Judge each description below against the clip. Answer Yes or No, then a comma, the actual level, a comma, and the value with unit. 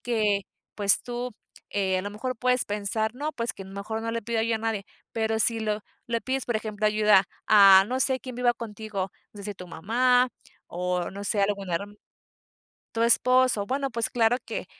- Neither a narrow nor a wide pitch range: Yes, average, 3.1 semitones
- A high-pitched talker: Yes, high, 220 Hz